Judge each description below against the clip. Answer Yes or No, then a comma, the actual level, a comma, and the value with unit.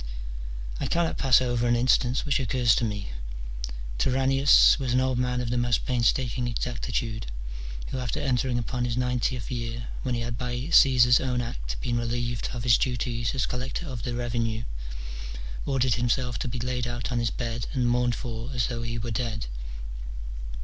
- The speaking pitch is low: Yes, low, 120 Hz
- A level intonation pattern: Yes, narrow, 1.4 semitones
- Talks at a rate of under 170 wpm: No, average, 185 wpm